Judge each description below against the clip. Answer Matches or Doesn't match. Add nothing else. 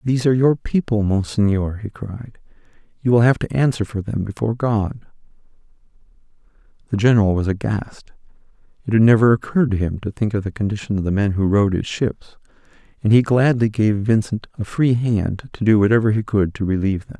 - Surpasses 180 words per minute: Matches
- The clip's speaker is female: Doesn't match